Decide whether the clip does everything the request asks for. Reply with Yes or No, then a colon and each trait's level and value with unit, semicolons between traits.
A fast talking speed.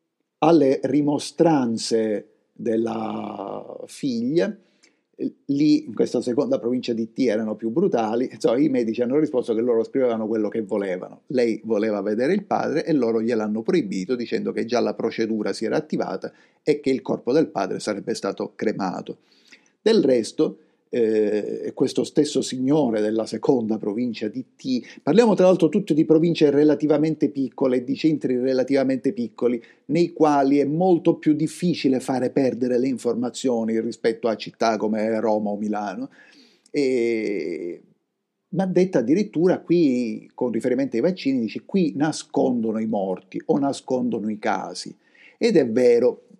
No: average, 145 wpm